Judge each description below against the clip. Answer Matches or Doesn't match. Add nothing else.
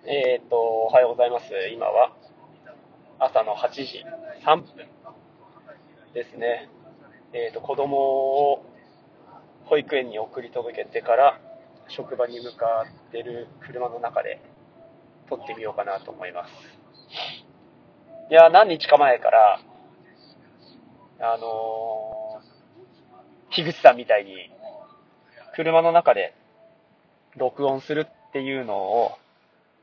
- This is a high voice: Doesn't match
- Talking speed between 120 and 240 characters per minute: Matches